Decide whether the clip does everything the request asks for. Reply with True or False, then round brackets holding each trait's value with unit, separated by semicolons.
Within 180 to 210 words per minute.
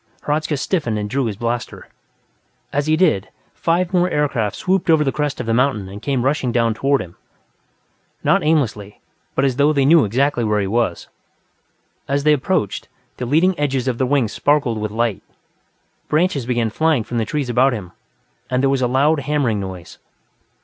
True (185 wpm)